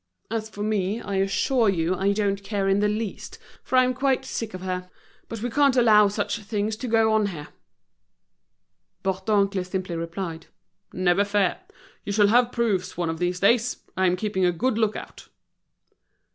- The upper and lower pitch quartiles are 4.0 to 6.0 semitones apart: No, average, 3.1 semitones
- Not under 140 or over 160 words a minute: No, average, 175 wpm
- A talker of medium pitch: No, high, 205 Hz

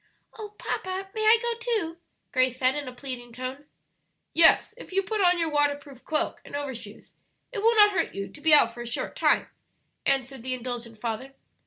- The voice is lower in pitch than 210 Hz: No, very high, 285 Hz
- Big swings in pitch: Yes, wide, 7.3 semitones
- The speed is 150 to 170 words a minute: No, average, 195 wpm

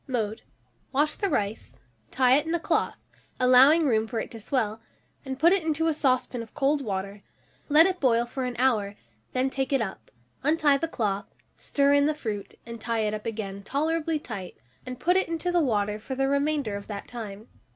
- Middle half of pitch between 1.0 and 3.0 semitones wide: No, wide, 5.5 semitones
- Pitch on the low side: No, very high, 255 Hz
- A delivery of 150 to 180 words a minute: No, fast, 205 wpm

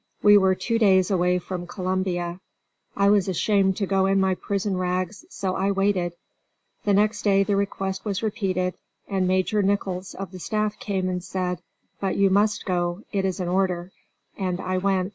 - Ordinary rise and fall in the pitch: No, narrow, 1.5 semitones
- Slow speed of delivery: No, average, 180 wpm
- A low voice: No, high, 190 Hz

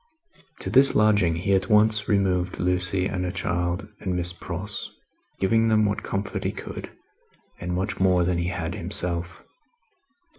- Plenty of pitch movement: No, average, 2.7 semitones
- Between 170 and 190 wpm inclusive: No, average, 155 wpm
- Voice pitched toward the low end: Yes, very low, 90 Hz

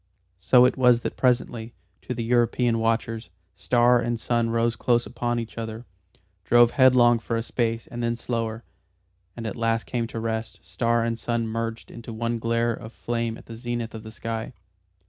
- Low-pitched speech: Yes, low, 115 Hz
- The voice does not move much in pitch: Yes, narrow, 0.9 semitones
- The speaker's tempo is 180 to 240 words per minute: Yes, average, 185 wpm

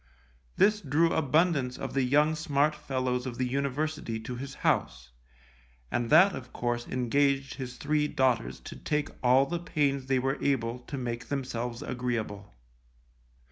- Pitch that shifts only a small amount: No, average, 3.2 semitones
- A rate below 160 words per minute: Yes, average, 150 wpm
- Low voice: Yes, low, 130 Hz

